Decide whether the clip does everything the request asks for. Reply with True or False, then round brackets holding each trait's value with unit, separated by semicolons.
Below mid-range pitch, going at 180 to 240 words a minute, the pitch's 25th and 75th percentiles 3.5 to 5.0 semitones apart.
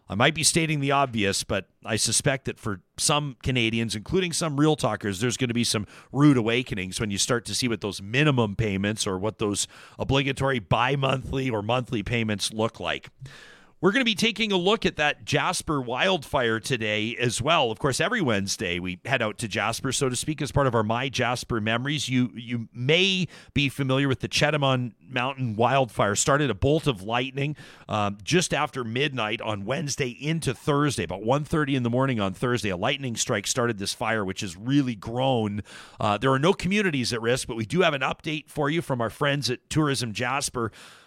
True (125 Hz; 200 wpm; 4.3 semitones)